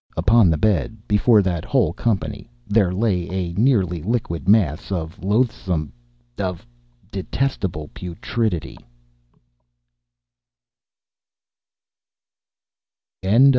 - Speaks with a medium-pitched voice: No, very low, 95 Hz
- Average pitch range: Yes, average, 4.6 semitones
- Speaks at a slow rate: Yes, slow, 75 wpm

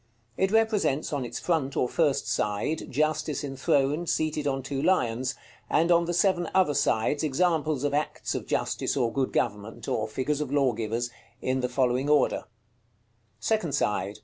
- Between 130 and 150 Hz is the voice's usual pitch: Yes, medium, 140 Hz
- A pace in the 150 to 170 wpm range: Yes, average, 160 wpm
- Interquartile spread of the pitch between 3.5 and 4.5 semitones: Yes, average, 3.9 semitones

